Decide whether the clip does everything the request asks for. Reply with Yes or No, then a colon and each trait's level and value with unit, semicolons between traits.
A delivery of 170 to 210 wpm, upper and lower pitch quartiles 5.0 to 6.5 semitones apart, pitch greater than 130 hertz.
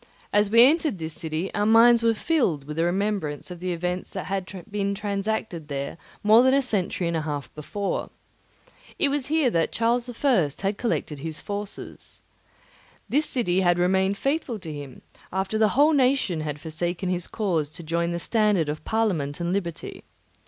Yes: average, 180 wpm; average, 5.3 semitones; high, 190 Hz